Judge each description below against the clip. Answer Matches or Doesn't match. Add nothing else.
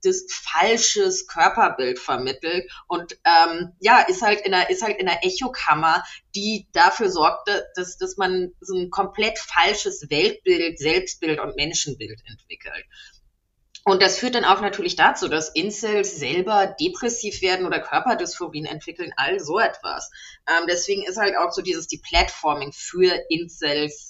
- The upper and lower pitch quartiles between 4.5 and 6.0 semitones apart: Matches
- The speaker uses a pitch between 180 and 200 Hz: Matches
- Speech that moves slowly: Doesn't match